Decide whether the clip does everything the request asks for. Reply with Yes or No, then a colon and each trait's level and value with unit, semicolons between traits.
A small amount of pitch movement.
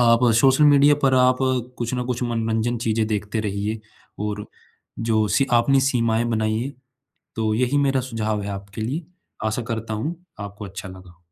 No: average, 3.0 semitones